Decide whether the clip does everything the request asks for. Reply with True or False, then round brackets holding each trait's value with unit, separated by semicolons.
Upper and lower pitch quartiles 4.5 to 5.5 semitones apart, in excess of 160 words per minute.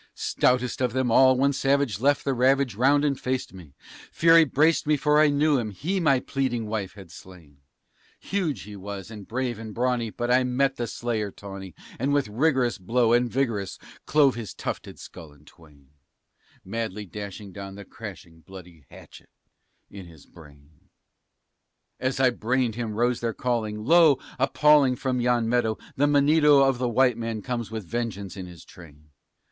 True (5.0 semitones; 175 wpm)